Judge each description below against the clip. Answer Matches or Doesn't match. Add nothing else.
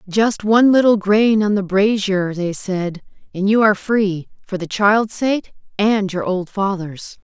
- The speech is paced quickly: Doesn't match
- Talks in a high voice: Matches